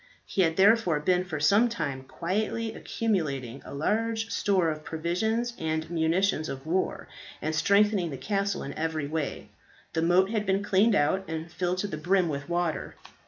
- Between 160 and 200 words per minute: Yes, average, 170 wpm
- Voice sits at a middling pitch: Yes, medium, 175 Hz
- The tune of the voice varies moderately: Yes, average, 4.3 semitones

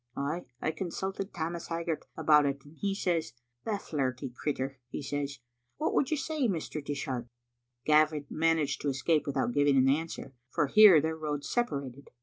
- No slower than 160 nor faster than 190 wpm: Yes, average, 170 wpm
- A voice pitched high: No, medium, 150 Hz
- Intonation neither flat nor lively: Yes, average, 3.3 semitones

